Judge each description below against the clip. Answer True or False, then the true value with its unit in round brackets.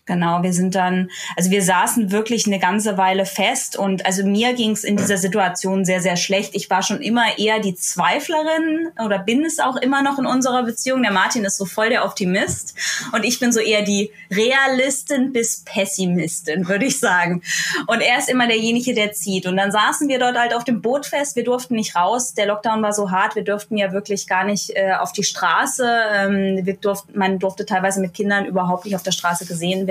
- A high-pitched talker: True (205 Hz)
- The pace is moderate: False (220 wpm)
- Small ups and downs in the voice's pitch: False (3.7 semitones)